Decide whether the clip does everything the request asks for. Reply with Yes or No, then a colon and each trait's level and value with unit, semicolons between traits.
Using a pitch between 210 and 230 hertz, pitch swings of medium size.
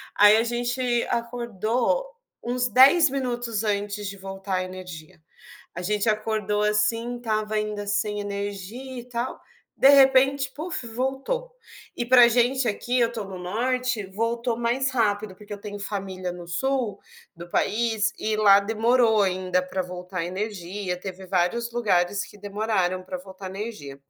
Yes: high, 215 Hz; average, 3.8 semitones